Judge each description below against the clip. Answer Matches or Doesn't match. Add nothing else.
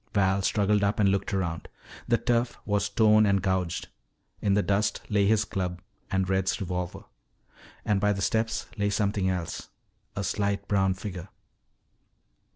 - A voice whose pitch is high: Doesn't match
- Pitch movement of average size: Doesn't match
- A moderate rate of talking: Matches